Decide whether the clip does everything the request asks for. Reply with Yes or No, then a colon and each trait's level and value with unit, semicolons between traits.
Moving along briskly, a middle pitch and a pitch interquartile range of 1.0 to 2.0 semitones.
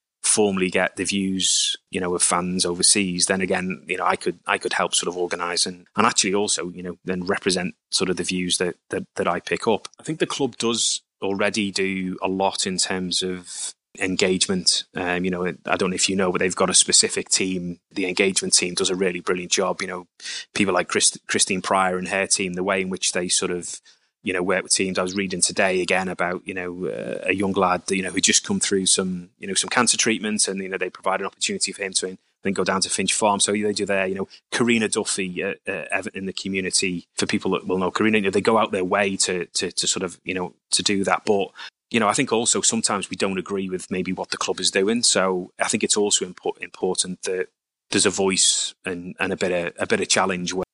No: fast, 250 wpm; very low, 95 Hz; narrow, 1.3 semitones